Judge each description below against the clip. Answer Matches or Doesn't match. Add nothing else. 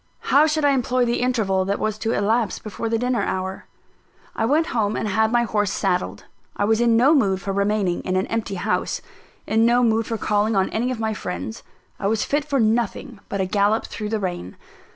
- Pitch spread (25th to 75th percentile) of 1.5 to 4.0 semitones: Matches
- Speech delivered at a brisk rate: Matches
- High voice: Matches